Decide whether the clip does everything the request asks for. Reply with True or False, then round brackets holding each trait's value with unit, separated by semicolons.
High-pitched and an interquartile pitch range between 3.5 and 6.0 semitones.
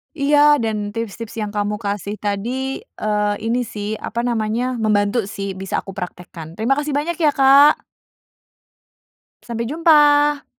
True (230 Hz; 5.2 semitones)